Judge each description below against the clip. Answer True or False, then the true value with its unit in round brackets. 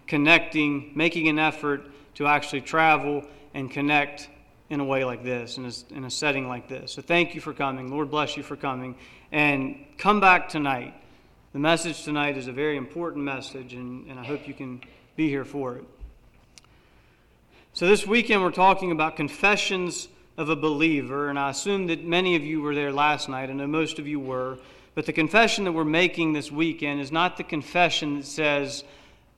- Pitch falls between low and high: True (145 Hz)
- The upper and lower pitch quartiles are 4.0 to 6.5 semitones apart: False (2.7 semitones)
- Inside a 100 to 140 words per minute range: False (190 wpm)